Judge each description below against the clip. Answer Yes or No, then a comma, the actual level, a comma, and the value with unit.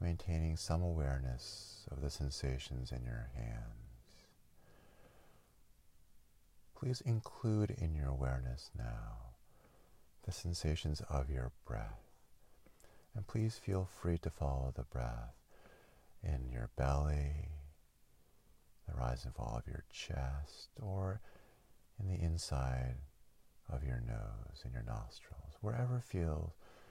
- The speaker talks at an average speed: No, slow, 110 wpm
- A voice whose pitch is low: Yes, very low, 75 Hz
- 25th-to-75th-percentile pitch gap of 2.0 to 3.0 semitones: No, wide, 6.1 semitones